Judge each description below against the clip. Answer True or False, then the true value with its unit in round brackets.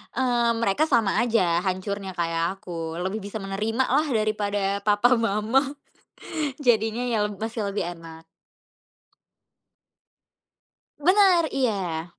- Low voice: False (210 Hz)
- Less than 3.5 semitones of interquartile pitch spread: False (3.8 semitones)